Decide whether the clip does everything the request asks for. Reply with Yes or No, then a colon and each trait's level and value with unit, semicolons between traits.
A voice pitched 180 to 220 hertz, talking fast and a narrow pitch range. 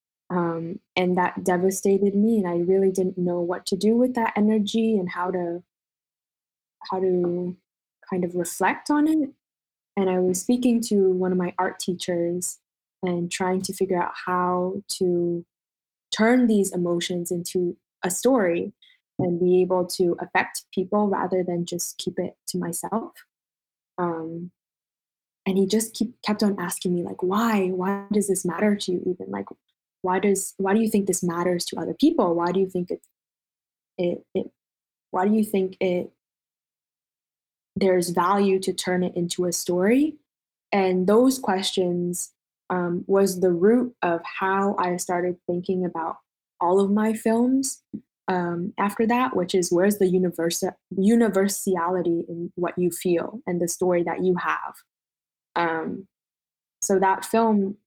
No: medium, 185 Hz; average, 160 wpm; narrow, 2.1 semitones